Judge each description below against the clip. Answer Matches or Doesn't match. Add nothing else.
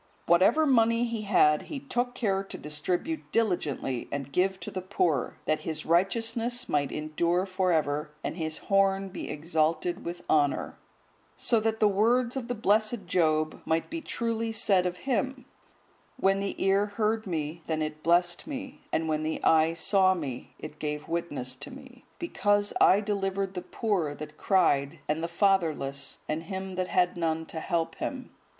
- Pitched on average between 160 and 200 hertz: Matches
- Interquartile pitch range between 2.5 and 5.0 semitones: Doesn't match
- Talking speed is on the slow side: Doesn't match